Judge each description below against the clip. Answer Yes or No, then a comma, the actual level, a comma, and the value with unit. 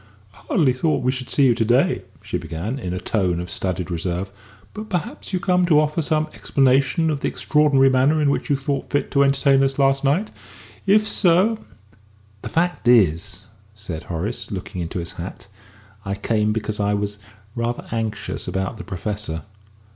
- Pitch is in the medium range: No, low, 120 Hz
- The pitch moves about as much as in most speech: No, wide, 6.0 semitones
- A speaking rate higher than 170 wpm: Yes, average, 185 wpm